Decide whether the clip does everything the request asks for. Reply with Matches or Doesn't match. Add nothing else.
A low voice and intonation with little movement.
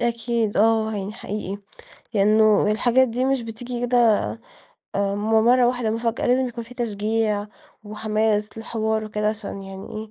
Doesn't match